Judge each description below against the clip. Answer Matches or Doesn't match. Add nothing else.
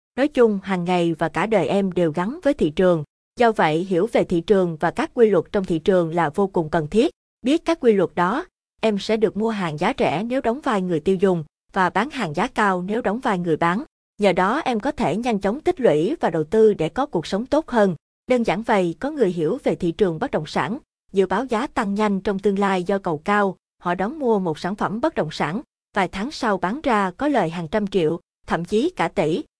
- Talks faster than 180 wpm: Matches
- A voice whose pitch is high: Matches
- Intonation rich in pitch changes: Doesn't match